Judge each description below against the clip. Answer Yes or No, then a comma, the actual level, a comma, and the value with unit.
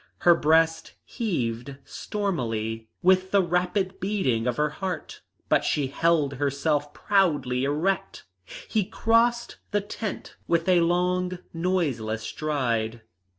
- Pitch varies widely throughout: Yes, wide, 5.9 semitones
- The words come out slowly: Yes, slow, 115 wpm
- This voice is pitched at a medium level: Yes, medium, 165 Hz